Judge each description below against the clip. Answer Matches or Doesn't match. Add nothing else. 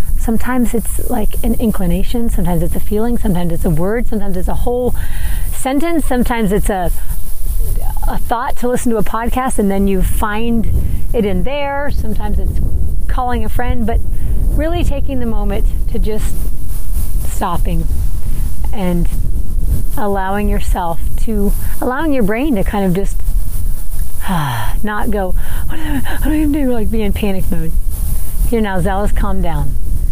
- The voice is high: Matches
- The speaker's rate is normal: Matches